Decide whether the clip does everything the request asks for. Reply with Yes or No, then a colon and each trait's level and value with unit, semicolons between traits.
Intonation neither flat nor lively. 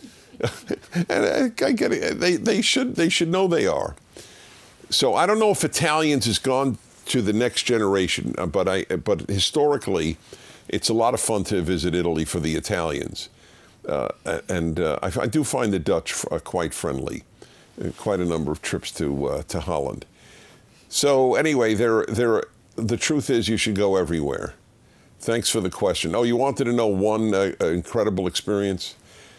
No: wide, 7.9 semitones